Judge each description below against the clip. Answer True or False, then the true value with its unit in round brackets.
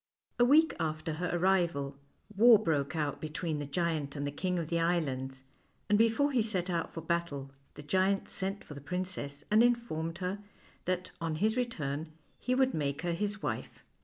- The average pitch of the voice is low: False (170 Hz)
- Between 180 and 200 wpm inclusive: True (185 wpm)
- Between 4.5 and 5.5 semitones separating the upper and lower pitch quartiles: True (5.0 semitones)